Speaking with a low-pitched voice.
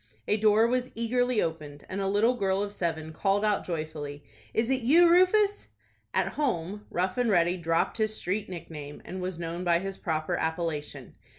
No: high, 190 Hz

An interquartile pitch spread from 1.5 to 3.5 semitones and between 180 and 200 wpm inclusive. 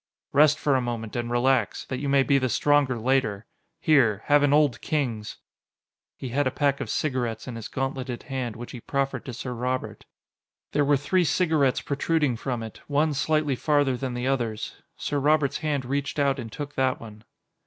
Yes: average, 3.0 semitones; average, 190 wpm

